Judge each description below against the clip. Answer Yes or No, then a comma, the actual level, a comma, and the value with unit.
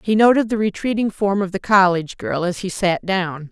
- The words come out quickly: Yes, fast, 220 wpm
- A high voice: Yes, high, 195 Hz